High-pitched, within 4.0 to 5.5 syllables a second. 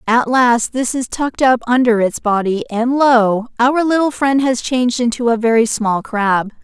Yes: high, 240 Hz; 4.6 syllables/s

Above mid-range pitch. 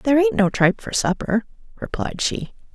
Yes: high, 215 Hz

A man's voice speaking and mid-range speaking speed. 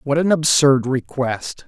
Yes: male; average, 145 wpm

